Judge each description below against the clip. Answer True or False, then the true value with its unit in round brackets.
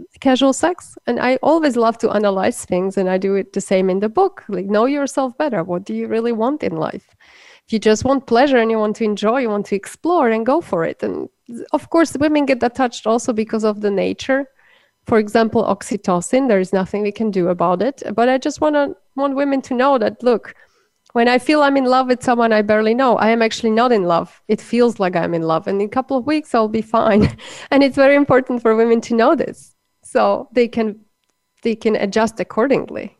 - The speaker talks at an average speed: False (230 wpm)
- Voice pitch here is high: True (230 Hz)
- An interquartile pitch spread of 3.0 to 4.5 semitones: True (4.0 semitones)